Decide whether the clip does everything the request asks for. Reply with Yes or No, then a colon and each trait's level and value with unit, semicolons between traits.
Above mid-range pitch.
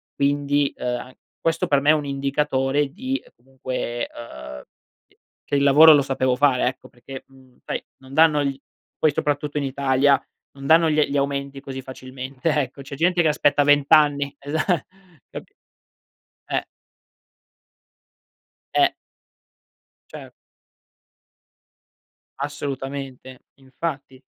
No: medium, 140 Hz